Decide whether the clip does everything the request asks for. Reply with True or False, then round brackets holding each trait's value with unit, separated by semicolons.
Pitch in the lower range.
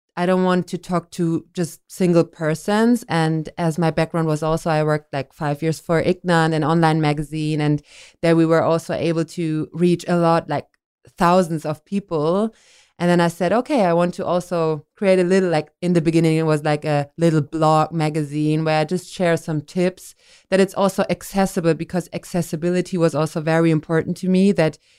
False (165 Hz)